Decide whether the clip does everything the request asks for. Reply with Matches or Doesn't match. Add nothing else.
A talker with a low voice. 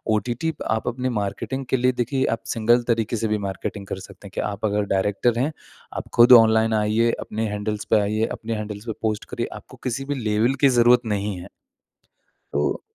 Matches